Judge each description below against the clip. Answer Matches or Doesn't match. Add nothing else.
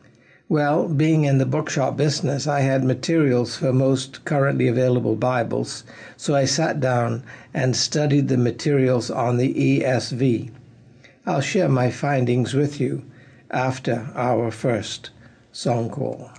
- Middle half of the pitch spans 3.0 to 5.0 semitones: Doesn't match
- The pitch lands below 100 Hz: Doesn't match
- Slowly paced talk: Matches